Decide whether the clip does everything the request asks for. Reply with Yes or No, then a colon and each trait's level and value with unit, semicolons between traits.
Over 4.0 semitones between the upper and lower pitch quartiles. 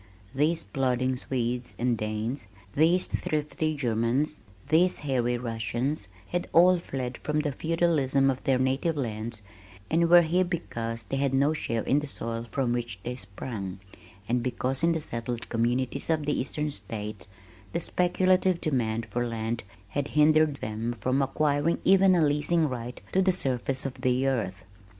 Yes: average, 4.7 semitones